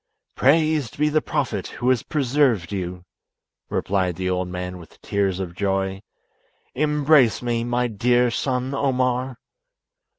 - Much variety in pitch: Yes, wide, 5.8 semitones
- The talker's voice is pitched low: Yes, low, 120 Hz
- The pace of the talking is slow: Yes, slow, 130 wpm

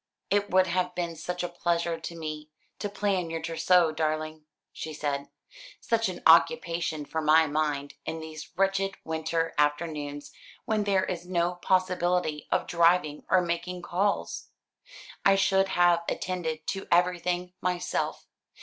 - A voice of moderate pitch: Yes, medium, 170 Hz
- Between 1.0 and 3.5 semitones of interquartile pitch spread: Yes, narrow, 2.5 semitones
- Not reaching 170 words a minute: Yes, average, 140 wpm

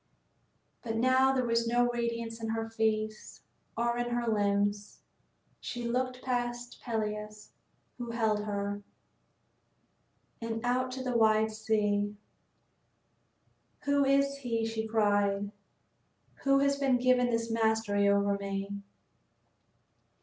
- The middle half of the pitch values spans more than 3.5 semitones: No, narrow, 2.4 semitones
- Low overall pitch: No, high, 225 Hz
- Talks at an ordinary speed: No, slow, 115 wpm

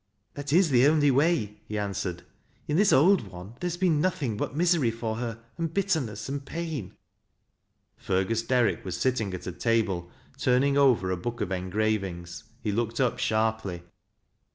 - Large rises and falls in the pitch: Yes, wide, 6.4 semitones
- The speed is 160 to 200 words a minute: Yes, average, 175 wpm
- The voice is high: No, low, 115 Hz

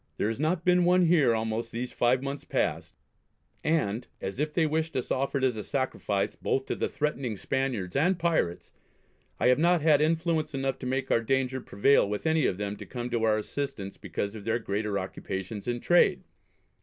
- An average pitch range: No, wide, 5.9 semitones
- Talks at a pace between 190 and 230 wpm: Yes, average, 195 wpm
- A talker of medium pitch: No, low, 130 Hz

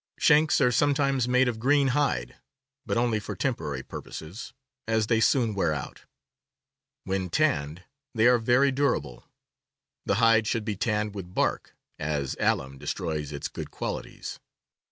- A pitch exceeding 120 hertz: No, low, 110 Hz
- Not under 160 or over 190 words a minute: No, average, 145 wpm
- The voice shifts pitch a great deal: Yes, wide, 7.1 semitones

